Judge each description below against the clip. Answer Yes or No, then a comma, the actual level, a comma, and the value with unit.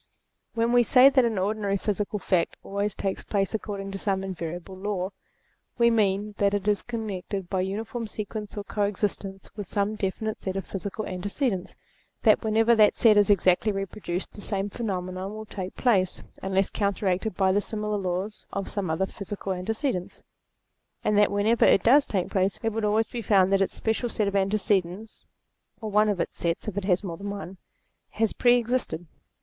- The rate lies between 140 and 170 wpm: No, average, 185 wpm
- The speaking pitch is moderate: No, high, 200 Hz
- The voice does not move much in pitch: Yes, narrow, 2.2 semitones